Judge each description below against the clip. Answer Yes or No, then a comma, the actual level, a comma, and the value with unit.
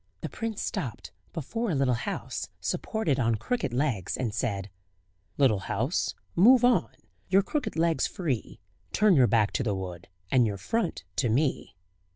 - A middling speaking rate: Yes, average, 160 wpm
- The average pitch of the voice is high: No, low, 135 Hz